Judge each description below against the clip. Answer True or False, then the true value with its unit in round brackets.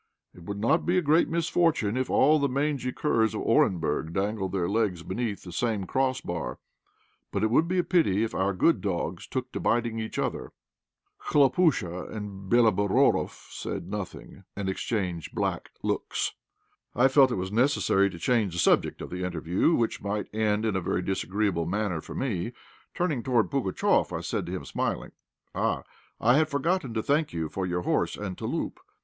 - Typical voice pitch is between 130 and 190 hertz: False (110 Hz)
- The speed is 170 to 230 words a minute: True (180 wpm)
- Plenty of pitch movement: True (5.8 semitones)